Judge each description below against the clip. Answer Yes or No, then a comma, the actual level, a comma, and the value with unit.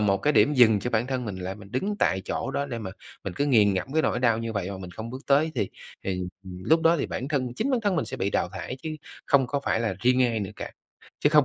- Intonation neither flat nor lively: No, wide, 5.9 semitones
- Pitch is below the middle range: Yes, low, 120 Hz